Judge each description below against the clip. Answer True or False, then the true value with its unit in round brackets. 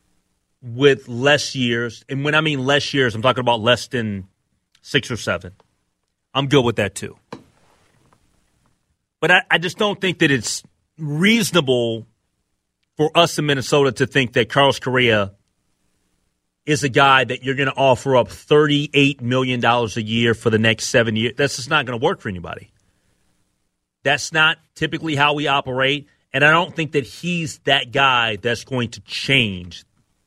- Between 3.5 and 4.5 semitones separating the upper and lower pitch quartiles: True (4.0 semitones)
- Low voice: True (130 Hz)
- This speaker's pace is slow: False (165 wpm)